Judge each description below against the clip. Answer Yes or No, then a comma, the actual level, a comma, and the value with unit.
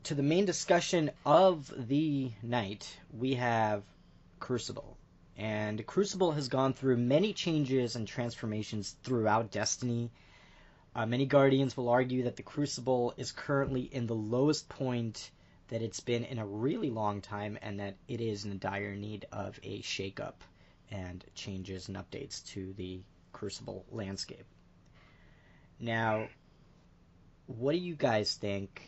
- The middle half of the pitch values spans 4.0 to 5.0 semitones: Yes, average, 4.7 semitones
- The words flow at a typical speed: Yes, average, 145 wpm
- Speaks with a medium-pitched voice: No, low, 115 Hz